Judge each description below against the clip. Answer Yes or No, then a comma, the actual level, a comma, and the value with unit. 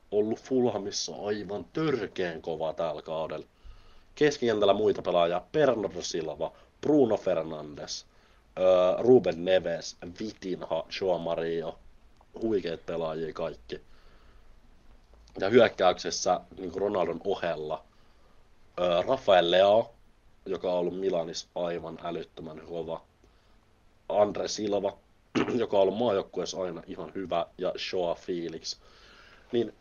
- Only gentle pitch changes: No, average, 3.9 semitones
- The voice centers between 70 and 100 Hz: Yes, very low, 95 Hz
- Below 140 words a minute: Yes, average, 100 wpm